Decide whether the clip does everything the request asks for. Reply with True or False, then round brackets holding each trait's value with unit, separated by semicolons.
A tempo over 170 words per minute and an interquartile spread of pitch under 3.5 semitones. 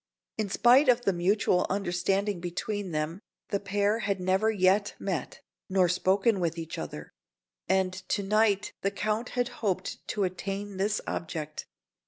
False (160 wpm; 2.4 semitones)